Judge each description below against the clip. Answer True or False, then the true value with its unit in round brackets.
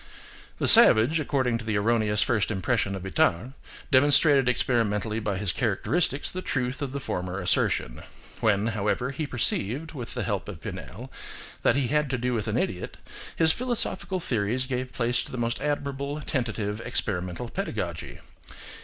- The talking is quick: False (160 wpm)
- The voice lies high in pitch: False (120 Hz)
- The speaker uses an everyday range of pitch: True (4.7 semitones)